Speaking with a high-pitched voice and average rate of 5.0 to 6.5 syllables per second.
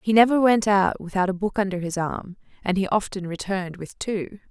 Yes: high, 195 Hz; 5.4 syllables/s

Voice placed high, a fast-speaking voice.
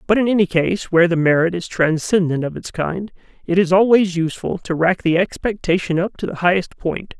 No: medium, 180 Hz; fast, 210 wpm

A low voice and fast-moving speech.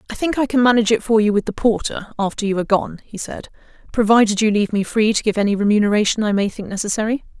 No: high, 215 Hz; fast, 245 wpm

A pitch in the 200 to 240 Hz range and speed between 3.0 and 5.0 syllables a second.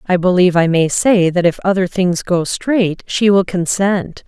No: medium, 185 Hz; 4.4 syllables/s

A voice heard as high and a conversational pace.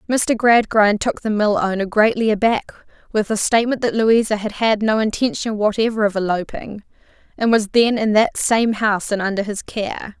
Yes: high, 215 Hz; average, 180 wpm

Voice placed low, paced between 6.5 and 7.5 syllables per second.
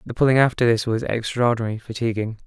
Yes: low, 115 Hz; 7.0 syllables/s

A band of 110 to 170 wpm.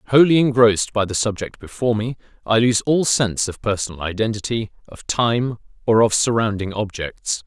Yes: average, 160 wpm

